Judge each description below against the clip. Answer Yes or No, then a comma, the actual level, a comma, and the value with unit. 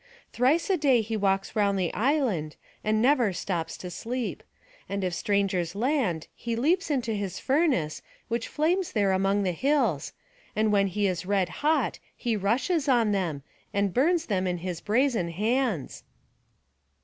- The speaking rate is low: No, average, 160 wpm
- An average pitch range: No, wide, 5.7 semitones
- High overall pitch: Yes, high, 210 Hz